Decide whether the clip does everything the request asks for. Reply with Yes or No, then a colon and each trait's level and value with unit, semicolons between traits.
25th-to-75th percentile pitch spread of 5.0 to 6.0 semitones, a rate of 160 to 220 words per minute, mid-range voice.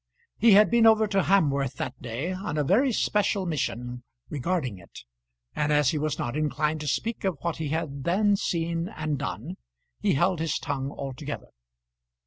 Yes: average, 5.3 semitones; average, 175 wpm; medium, 155 Hz